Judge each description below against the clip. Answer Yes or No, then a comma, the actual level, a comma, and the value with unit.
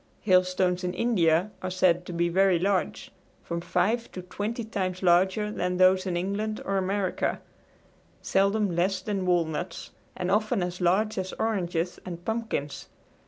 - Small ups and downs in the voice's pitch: Yes, narrow, 2.3 semitones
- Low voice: No, medium, 185 Hz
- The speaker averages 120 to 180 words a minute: Yes, average, 150 wpm